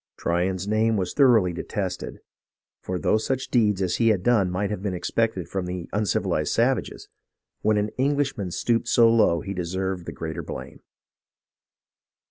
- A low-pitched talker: Yes, low, 100 Hz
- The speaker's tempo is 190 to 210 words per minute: No, average, 155 wpm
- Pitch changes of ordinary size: Yes, average, 3.9 semitones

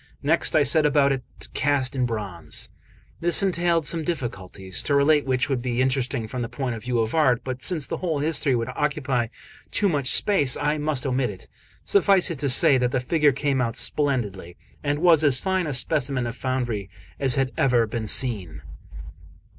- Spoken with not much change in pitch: No, average, 3.6 semitones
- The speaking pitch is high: No, low, 135 Hz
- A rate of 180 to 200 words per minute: Yes, average, 195 wpm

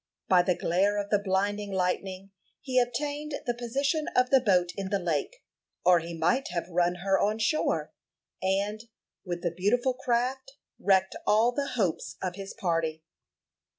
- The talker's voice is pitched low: No, high, 200 Hz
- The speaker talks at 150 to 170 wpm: Yes, average, 160 wpm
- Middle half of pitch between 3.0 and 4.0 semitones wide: No, average, 5.2 semitones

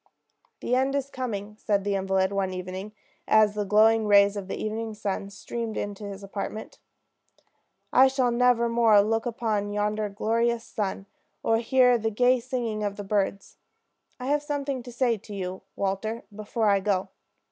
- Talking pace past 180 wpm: No, average, 170 wpm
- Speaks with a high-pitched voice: Yes, high, 215 Hz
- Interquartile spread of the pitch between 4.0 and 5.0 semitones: No, average, 2.9 semitones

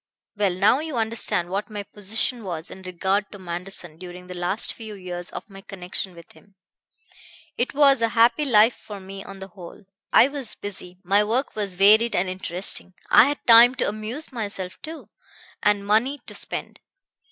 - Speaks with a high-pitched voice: Yes, high, 205 Hz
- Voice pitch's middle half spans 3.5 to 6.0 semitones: Yes, average, 3.8 semitones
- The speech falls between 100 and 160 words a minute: No, average, 180 wpm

